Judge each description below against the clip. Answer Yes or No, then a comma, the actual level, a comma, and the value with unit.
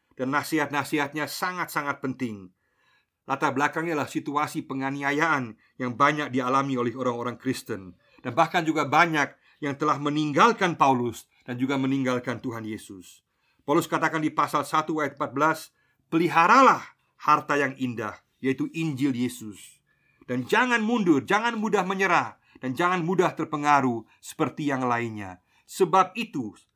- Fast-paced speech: No, average, 130 wpm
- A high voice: No, medium, 140 Hz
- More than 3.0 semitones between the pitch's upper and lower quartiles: Yes, average, 3.9 semitones